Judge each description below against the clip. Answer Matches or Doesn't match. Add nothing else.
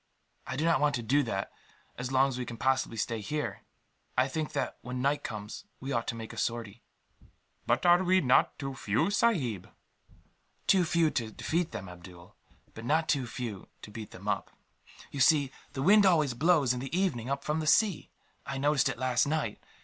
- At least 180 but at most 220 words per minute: Matches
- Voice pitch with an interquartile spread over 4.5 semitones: Matches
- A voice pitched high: Doesn't match